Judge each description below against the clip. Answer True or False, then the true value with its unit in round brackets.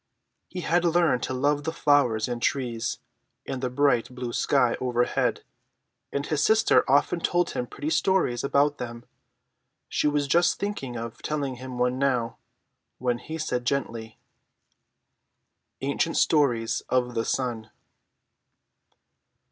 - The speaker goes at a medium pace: False (130 wpm)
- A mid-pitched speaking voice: False (130 Hz)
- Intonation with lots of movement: False (3.3 semitones)